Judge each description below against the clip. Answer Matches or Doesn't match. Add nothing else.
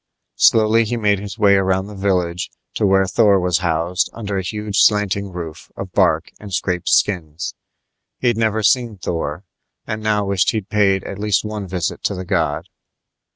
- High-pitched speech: Doesn't match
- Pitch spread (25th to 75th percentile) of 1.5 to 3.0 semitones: Matches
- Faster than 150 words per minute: Matches